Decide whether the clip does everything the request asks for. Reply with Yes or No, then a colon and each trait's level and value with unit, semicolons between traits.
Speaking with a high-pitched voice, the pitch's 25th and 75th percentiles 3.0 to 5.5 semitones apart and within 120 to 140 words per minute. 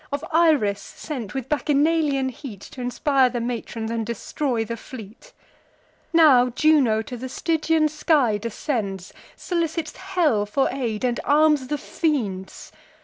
Yes: very high, 265 Hz; average, 5.1 semitones; slow, 135 wpm